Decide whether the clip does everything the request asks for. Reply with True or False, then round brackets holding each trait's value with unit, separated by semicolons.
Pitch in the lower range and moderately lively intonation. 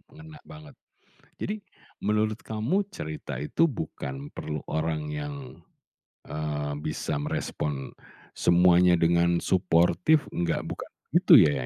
False (85 Hz; 5.9 semitones)